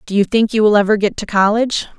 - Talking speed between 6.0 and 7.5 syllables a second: Yes, 6.8 syllables/s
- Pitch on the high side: Yes, high, 210 Hz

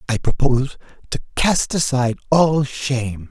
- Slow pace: Yes, slow, 125 wpm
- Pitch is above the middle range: No, low, 135 Hz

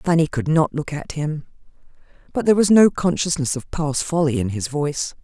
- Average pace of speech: Yes, average, 195 wpm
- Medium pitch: Yes, medium, 155 Hz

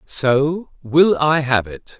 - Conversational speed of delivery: Yes, average, 150 wpm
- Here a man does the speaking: Yes, male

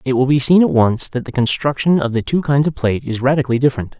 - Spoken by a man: Yes, male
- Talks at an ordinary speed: No, fast, 270 wpm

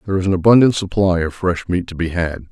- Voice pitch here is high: No, very low, 90 Hz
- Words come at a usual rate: No, fast, 260 wpm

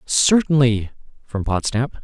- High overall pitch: No, low, 130 Hz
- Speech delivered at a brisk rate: No, slow, 90 wpm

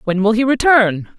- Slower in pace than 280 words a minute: Yes, average, 200 wpm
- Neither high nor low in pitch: No, high, 220 Hz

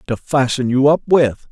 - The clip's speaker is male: Yes, male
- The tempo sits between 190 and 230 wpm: Yes, average, 200 wpm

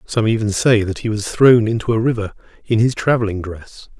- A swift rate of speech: Yes, fast, 210 wpm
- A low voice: Yes, low, 110 Hz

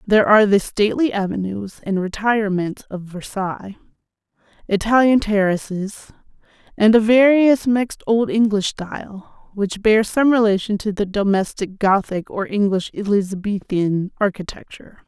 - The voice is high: Yes, high, 205 Hz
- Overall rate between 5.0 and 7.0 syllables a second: No, 4.8 syllables/s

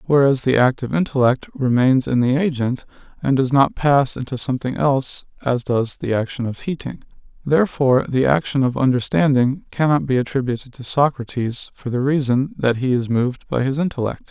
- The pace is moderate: Yes, average, 175 wpm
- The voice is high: No, low, 130 Hz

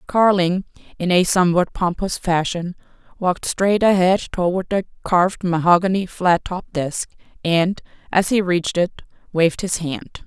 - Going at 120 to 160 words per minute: Yes, average, 140 wpm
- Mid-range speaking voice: Yes, medium, 180 Hz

